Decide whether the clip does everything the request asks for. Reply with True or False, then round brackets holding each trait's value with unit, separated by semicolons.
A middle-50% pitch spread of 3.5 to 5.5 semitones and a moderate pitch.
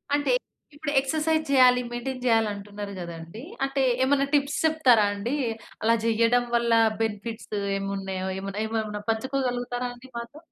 False (4.3 semitones; 235 Hz)